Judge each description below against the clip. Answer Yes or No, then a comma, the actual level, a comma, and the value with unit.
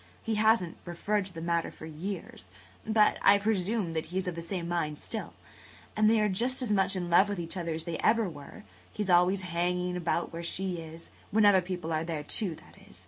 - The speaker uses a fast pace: Yes, fast, 220 wpm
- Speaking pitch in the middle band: Yes, medium, 180 Hz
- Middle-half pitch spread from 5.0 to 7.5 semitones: No, average, 3.5 semitones